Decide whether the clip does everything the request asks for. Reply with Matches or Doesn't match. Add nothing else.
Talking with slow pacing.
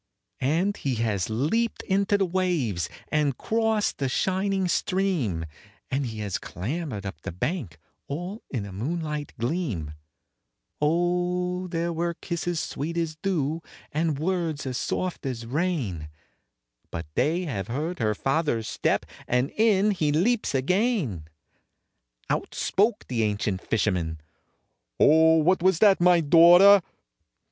Matches